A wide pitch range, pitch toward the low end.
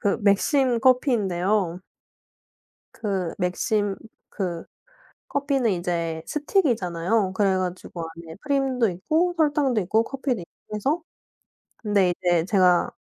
No: wide, 6.4 semitones; high, 205 Hz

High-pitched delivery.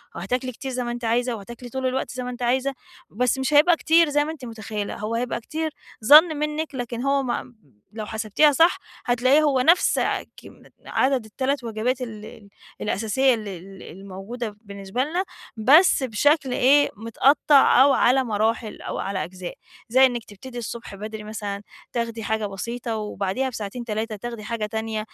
Yes: high, 240 Hz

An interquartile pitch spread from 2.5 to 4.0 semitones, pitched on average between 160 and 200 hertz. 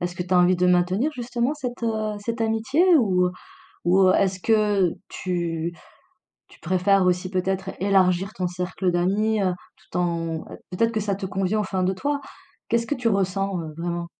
Yes: average, 3.2 semitones; high, 190 Hz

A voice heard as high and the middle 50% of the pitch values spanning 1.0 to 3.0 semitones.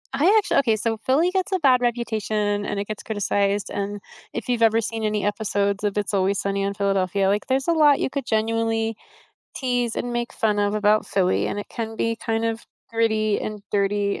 Yes: high, 220 Hz; average, 2.7 semitones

